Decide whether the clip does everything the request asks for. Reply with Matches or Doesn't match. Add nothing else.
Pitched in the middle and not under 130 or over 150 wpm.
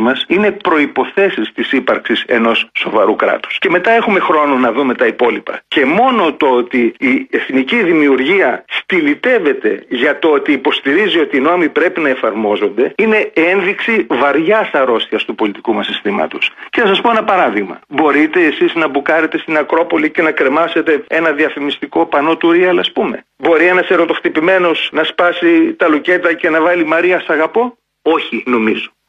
Doesn't match